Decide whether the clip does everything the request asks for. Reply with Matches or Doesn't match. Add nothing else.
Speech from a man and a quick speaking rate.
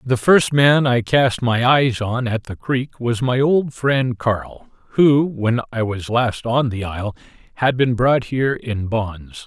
Doesn't match